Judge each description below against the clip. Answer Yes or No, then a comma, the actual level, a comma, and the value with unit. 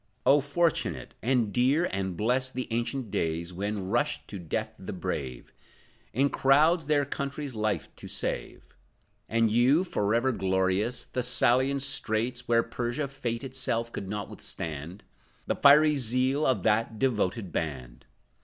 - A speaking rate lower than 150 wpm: Yes, slow, 135 wpm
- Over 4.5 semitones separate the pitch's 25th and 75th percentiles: Yes, average, 5.1 semitones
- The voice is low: Yes, low, 120 Hz